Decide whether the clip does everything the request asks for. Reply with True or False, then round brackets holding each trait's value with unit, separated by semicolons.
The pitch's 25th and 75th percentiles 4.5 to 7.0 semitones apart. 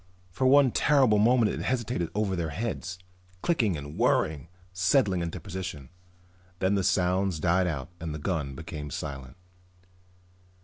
True (5.3 semitones)